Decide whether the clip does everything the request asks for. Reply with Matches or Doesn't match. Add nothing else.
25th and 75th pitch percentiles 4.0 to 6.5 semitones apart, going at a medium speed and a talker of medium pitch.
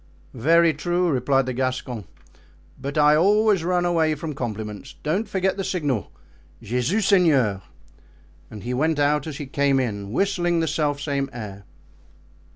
Matches